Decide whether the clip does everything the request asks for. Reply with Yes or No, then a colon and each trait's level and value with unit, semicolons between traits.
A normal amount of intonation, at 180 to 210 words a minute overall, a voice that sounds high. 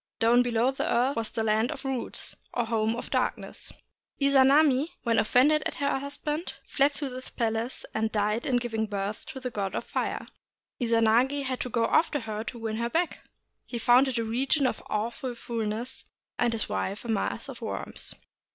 Yes: average, 3.2 semitones; average, 190 wpm; high, 240 Hz